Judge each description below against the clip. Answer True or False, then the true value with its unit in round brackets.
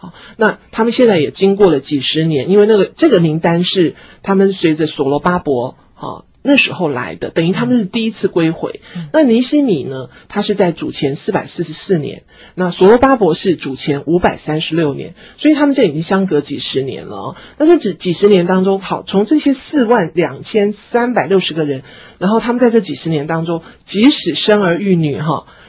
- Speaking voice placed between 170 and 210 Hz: True (190 Hz)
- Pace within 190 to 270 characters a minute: False (310 characters per minute)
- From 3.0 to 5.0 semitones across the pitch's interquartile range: False (5.6 semitones)